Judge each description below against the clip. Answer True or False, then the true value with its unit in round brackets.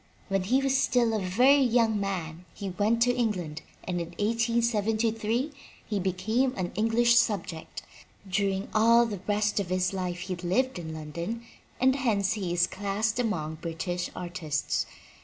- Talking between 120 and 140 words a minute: False (160 wpm)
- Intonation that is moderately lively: True (4.4 semitones)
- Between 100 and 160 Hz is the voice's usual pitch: False (205 Hz)